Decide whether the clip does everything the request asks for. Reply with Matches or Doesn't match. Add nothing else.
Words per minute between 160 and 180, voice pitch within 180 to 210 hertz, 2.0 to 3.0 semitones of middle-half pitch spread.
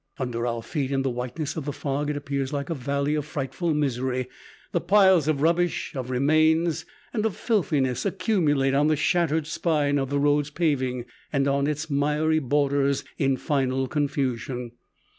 Doesn't match